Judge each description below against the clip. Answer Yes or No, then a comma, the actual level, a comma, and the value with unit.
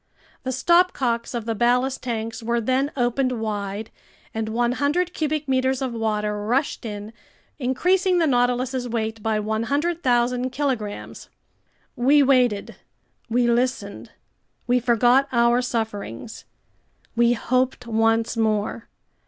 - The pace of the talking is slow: Yes, slow, 115 wpm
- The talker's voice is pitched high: Yes, high, 240 Hz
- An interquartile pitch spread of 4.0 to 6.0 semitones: No, average, 2.8 semitones